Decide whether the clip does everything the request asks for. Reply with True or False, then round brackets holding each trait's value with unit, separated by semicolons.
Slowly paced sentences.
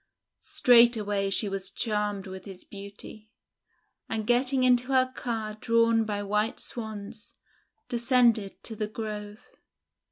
True (120 wpm)